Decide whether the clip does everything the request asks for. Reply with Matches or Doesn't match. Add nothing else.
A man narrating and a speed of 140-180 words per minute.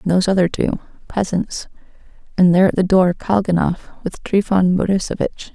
Doesn't match